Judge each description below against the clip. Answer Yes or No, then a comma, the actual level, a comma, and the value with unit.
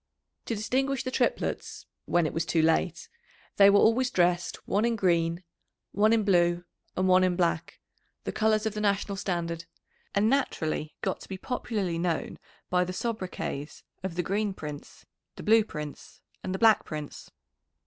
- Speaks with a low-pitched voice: No, medium, 185 Hz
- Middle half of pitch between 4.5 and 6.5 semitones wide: No, average, 4.0 semitones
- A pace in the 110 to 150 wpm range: No, average, 170 wpm